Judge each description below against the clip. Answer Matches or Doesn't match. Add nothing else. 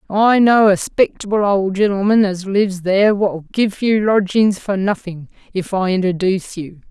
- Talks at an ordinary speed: Matches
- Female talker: Matches